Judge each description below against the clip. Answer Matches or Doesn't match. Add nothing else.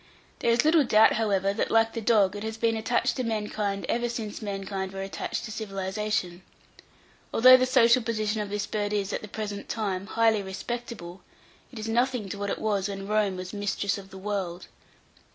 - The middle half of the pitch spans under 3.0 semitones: Matches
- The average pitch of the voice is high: Matches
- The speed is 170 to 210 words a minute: Matches